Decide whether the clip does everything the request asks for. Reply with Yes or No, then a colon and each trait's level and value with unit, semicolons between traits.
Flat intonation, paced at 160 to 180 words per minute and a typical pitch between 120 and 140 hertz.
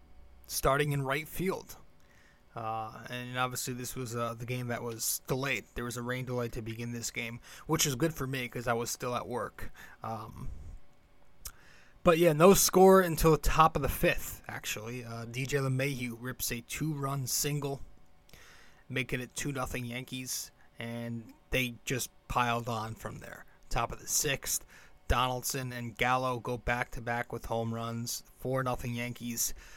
Yes: narrow, 2.3 semitones; average, 165 wpm; low, 125 Hz